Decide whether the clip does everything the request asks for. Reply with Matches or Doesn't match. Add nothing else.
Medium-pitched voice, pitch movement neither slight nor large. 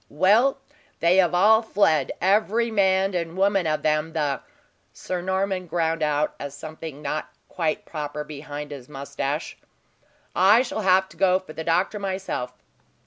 Matches